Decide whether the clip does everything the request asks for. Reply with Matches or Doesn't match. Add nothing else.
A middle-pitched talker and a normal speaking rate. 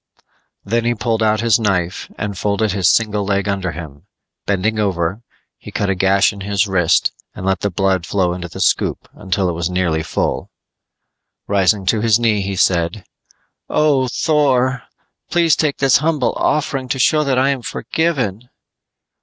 Doesn't match